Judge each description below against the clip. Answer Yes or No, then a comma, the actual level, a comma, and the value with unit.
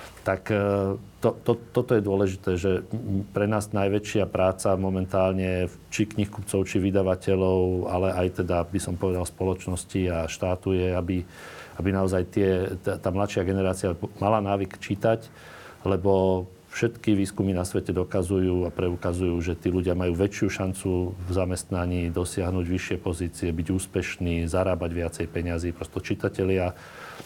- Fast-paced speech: No, average, 135 wpm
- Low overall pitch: Yes, very low, 95 Hz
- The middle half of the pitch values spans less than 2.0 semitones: Yes, narrow, 1.6 semitones